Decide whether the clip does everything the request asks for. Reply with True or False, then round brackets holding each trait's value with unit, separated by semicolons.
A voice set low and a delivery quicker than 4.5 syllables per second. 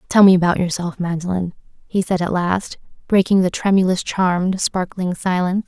False (185 Hz; 5.3 syllables/s)